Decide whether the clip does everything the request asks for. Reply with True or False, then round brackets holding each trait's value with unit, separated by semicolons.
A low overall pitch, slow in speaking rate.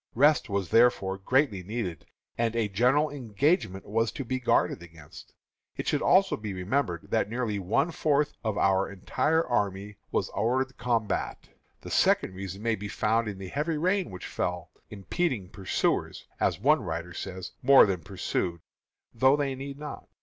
False (110 Hz; 165 wpm)